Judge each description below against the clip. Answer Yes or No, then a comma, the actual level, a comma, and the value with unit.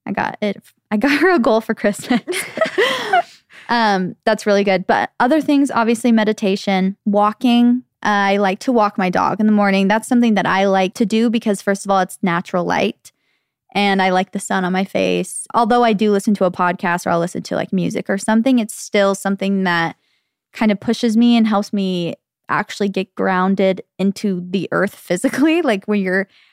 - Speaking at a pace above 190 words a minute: Yes, average, 200 wpm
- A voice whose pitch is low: No, high, 205 Hz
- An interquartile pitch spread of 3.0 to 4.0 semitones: Yes, average, 3.3 semitones